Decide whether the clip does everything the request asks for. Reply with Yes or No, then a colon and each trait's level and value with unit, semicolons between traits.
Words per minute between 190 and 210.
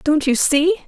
Yes: fast, 205 wpm